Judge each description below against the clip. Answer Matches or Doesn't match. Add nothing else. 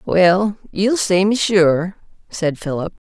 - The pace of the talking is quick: Doesn't match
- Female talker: Matches